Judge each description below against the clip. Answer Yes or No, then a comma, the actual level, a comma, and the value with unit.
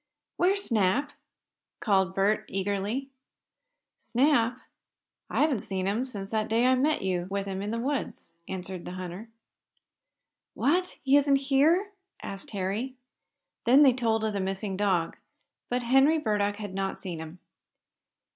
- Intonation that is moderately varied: No, wide, 5.7 semitones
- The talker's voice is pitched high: Yes, high, 215 Hz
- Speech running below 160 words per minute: Yes, average, 145 wpm